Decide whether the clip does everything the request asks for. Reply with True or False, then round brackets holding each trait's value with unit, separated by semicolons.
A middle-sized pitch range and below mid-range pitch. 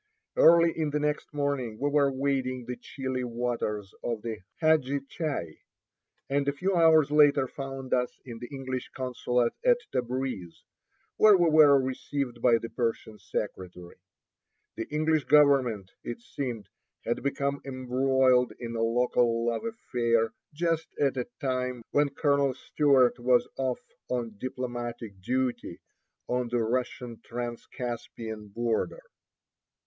True (3.1 semitones; 130 Hz)